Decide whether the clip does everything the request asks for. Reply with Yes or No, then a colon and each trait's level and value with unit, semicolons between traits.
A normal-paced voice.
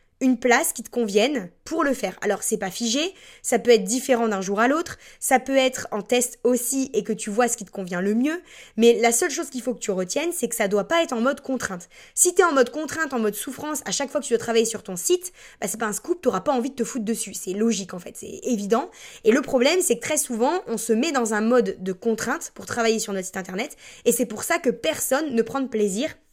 No: fast, 275 wpm